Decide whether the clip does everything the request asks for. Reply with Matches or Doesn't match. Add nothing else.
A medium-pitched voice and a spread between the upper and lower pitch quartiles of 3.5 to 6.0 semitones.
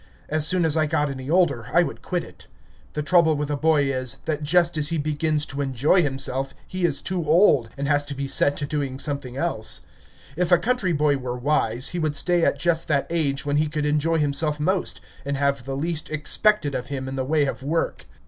Doesn't match